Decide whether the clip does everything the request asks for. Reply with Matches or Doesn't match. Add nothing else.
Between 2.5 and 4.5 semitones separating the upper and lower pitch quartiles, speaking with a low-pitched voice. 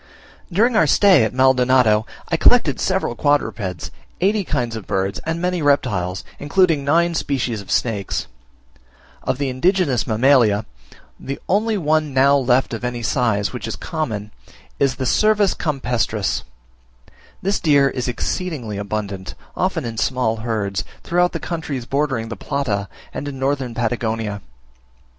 Doesn't match